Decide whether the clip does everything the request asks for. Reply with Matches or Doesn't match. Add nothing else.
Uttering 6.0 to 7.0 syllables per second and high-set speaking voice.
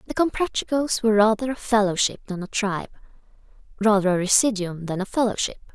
Matches